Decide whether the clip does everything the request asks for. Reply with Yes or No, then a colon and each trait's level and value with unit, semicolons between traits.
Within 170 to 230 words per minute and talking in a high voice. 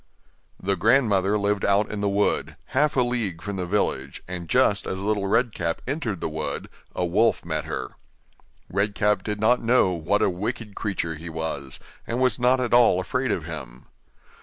No: average, 185 wpm; low, 100 Hz